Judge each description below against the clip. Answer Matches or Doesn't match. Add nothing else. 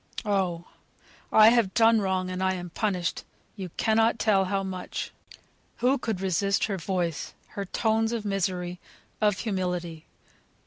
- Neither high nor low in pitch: Doesn't match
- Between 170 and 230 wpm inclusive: Doesn't match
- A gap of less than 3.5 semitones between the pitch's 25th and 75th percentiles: Matches